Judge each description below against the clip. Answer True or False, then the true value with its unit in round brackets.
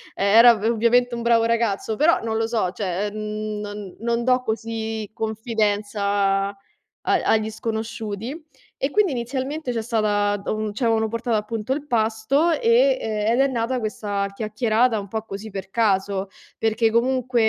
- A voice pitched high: True (225 Hz)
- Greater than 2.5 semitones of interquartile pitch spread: False (2.0 semitones)